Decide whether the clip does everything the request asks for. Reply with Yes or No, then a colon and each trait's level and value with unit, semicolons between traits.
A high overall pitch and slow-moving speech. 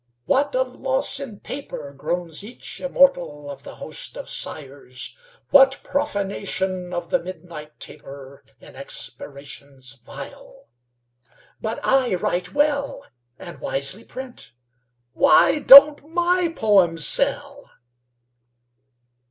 Yes: high, 205 Hz; slow, 105 wpm